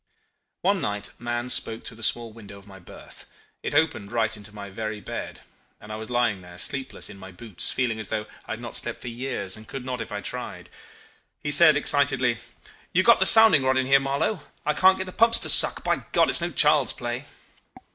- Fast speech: Yes, fast, 220 wpm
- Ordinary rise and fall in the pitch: Yes, average, 5.0 semitones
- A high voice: No, low, 120 Hz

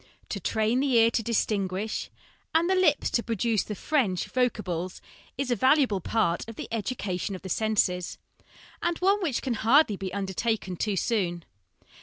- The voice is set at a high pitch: Yes, high, 220 Hz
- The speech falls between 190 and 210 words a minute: No, average, 170 wpm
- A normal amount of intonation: Yes, average, 4.9 semitones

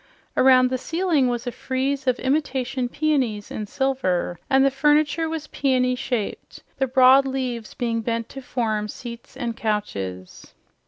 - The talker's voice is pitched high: Yes, very high, 255 Hz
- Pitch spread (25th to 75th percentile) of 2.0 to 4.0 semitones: Yes, average, 2.8 semitones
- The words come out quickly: No, average, 150 wpm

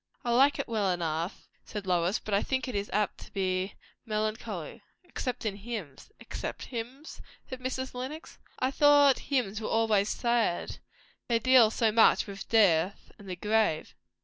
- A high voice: Yes, high, 220 Hz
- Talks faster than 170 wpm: No, average, 165 wpm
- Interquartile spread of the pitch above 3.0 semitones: Yes, average, 4.3 semitones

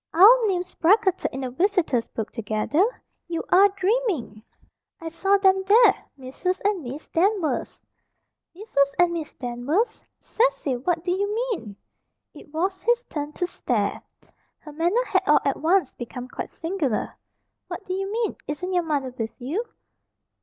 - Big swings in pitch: Yes, wide, 6.0 semitones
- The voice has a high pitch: Yes, very high, 350 Hz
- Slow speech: No, average, 155 wpm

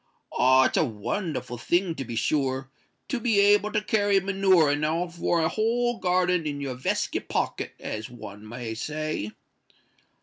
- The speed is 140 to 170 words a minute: Yes, average, 160 wpm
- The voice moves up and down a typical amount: No, wide, 7.1 semitones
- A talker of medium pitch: Yes, medium, 160 Hz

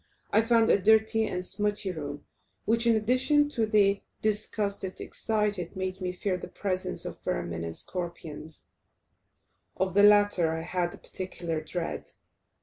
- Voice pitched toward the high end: Yes, high, 195 Hz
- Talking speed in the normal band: Yes, average, 150 wpm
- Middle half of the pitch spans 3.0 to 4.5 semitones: Yes, average, 3.4 semitones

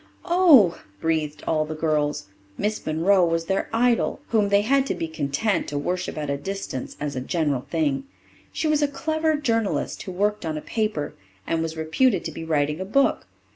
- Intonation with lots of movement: Yes, wide, 6.9 semitones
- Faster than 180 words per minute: Yes, average, 190 wpm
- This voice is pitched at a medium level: Yes, medium, 180 Hz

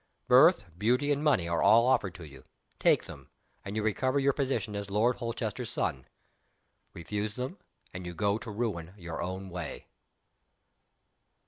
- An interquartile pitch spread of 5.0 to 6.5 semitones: Yes, average, 5.3 semitones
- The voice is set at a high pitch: No, low, 105 Hz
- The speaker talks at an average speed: Yes, average, 155 wpm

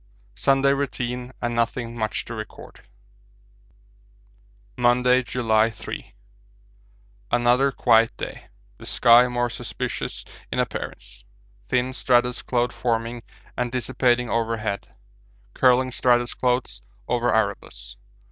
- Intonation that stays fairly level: Yes, narrow, 1.3 semitones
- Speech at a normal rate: No, slow, 100 wpm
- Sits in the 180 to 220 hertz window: No, low, 120 Hz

